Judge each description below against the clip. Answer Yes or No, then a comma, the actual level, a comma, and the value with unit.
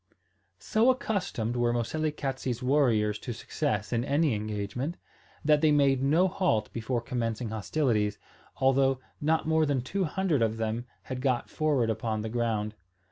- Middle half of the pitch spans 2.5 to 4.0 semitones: No, average, 5.1 semitones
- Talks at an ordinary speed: Yes, average, 145 wpm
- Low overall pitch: Yes, low, 125 Hz